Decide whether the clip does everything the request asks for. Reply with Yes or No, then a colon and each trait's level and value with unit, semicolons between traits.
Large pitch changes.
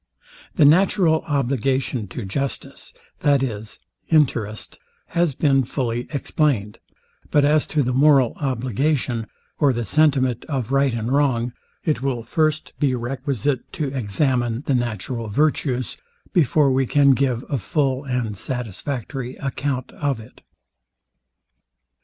No: average, 3.3 semitones